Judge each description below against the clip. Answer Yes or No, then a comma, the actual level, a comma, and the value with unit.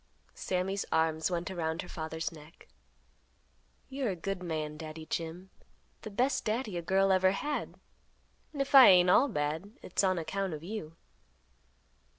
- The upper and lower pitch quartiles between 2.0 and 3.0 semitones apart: No, average, 3.6 semitones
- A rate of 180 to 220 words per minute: No, average, 155 wpm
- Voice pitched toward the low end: No, medium, 180 Hz